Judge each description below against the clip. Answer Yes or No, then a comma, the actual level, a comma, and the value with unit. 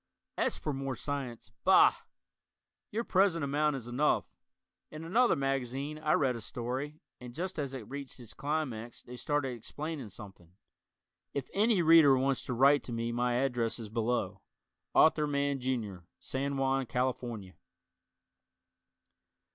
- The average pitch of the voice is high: No, low, 135 Hz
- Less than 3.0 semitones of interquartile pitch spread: No, average, 3.5 semitones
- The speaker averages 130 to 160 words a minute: Yes, average, 140 wpm